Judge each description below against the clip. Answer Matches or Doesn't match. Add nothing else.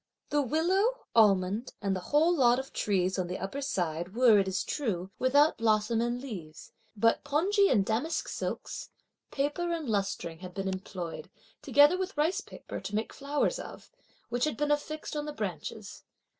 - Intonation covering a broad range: Matches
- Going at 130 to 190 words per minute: Matches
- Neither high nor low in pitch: Doesn't match